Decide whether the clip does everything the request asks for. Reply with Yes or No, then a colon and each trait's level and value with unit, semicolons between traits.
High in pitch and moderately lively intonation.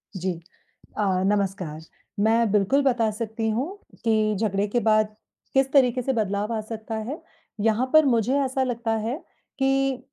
Yes: high, 225 Hz; average, 3.4 semitones